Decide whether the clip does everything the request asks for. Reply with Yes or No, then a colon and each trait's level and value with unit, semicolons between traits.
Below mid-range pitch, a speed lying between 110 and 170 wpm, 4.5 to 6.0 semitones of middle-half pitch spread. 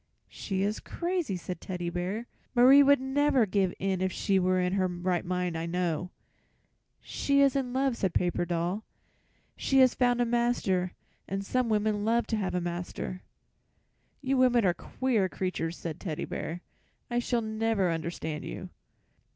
No: high, 195 Hz; average, 165 wpm; average, 5.3 semitones